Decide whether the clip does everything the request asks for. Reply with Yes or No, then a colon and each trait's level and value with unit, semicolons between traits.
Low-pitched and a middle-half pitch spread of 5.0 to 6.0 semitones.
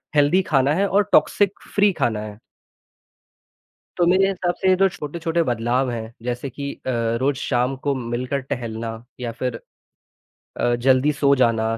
Yes: low, 130 Hz; wide, 5.6 semitones